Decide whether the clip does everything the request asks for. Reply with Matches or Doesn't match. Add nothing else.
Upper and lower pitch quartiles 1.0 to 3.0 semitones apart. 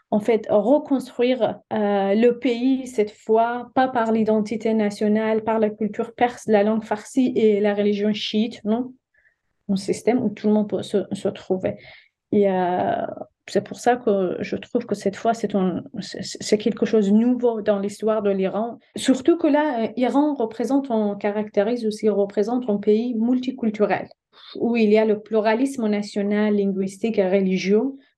Matches